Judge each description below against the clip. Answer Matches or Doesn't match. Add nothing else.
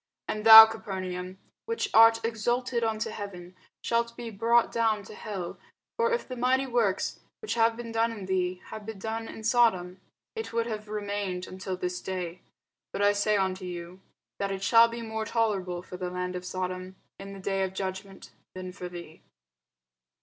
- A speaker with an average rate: Matches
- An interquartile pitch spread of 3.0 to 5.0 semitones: Matches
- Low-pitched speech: Doesn't match